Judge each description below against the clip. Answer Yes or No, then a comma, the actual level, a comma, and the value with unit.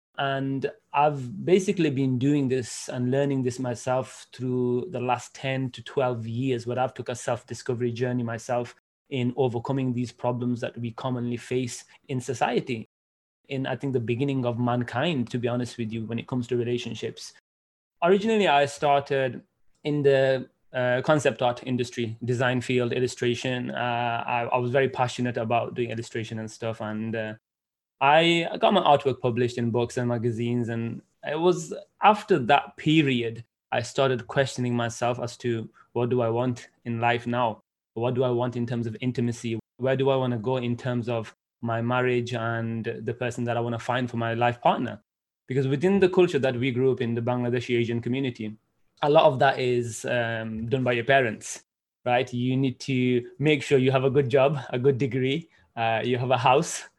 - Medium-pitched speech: No, low, 125 Hz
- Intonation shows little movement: Yes, narrow, 1.9 semitones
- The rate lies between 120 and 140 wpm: No, average, 185 wpm